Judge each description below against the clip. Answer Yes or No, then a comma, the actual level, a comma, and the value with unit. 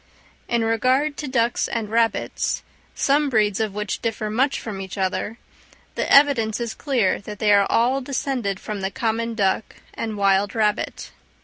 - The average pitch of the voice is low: No, high, 225 Hz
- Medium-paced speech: Yes, average, 165 wpm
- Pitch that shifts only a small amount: No, average, 3.3 semitones